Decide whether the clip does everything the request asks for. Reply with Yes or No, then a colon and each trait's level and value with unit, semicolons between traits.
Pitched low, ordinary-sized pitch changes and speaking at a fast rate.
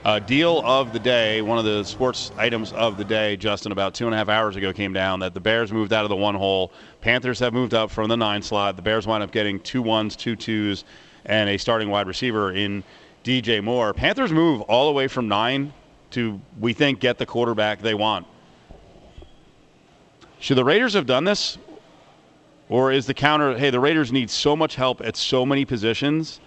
Yes: low, 115 Hz; average, 3.5 semitones; fast, 210 wpm